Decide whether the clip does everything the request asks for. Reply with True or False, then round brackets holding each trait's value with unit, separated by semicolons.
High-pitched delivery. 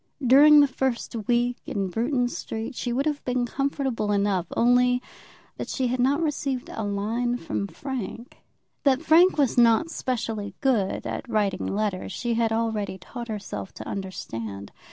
True (240 Hz)